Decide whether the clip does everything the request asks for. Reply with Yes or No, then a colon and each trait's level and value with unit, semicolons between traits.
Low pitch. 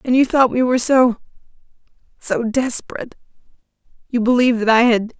No: high, 240 Hz